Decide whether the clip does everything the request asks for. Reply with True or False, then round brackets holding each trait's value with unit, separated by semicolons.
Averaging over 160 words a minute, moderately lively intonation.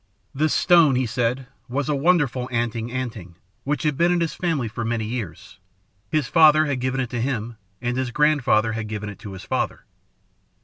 True (190 wpm; 4.6 semitones)